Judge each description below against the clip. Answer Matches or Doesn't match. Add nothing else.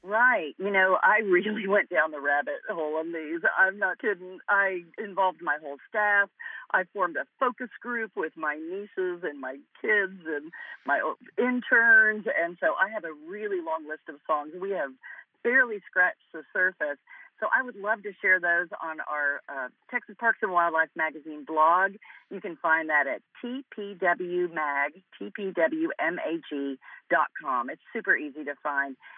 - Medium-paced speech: Matches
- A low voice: Doesn't match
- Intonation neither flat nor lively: Doesn't match